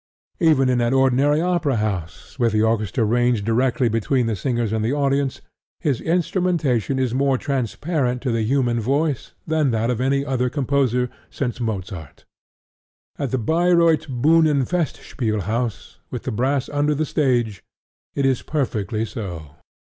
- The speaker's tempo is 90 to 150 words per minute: Yes, average, 145 wpm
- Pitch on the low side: Yes, low, 130 Hz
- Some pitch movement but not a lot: Yes, average, 4.0 semitones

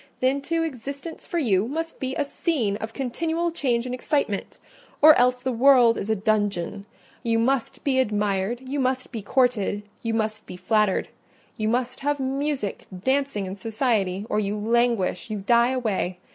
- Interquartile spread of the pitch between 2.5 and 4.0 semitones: No, average, 4.4 semitones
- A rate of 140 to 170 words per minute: Yes, average, 160 wpm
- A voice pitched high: Yes, high, 235 Hz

